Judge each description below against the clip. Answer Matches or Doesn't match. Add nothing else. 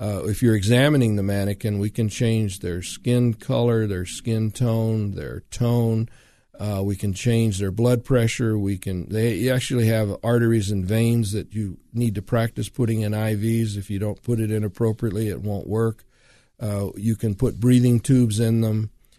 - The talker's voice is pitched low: Matches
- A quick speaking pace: Doesn't match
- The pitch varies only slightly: Matches